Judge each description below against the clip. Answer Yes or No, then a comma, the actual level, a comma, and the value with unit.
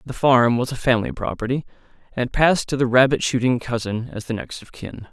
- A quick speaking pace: Yes, fast, 210 wpm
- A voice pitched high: No, low, 125 Hz